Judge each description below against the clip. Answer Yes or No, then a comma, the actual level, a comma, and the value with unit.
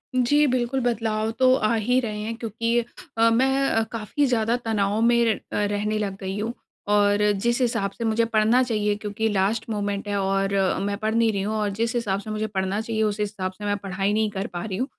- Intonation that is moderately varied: No, narrow, 2.3 semitones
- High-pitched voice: Yes, high, 215 Hz